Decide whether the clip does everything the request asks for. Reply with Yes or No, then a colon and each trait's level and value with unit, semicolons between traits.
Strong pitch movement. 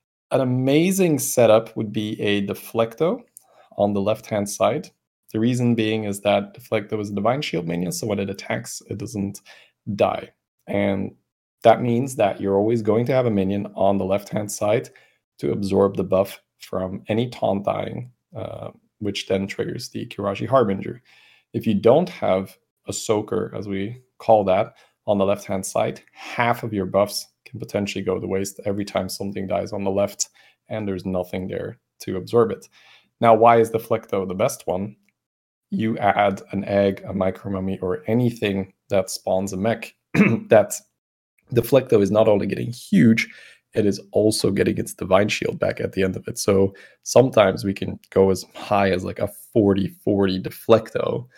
No: narrow, 2.6 semitones